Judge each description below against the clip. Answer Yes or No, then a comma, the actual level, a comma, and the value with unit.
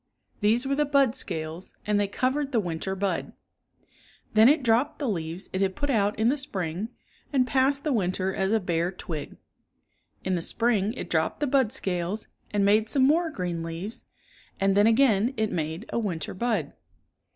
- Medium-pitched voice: No, high, 210 Hz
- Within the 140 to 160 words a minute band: No, average, 185 wpm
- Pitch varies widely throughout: Yes, wide, 5.8 semitones